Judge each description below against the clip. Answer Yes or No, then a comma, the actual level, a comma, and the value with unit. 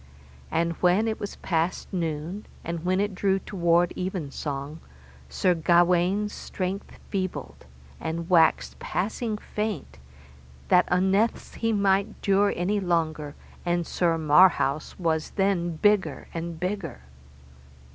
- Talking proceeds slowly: Yes, slow, 120 wpm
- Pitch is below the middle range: No, medium, 180 Hz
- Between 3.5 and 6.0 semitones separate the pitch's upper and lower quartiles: No, average, 3.1 semitones